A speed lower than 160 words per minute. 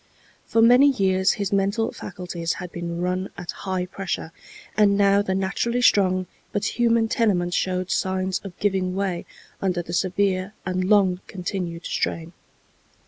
Yes: average, 145 wpm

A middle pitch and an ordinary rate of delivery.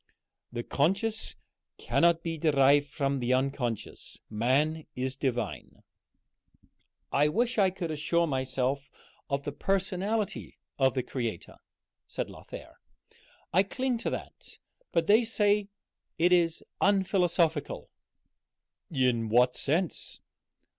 No: medium, 150 Hz; slow, 110 wpm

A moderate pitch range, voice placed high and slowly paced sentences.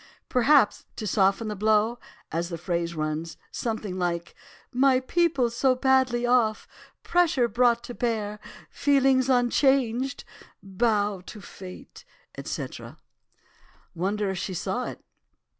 Yes: average, 4.9 semitones; high, 225 Hz; slow, 110 wpm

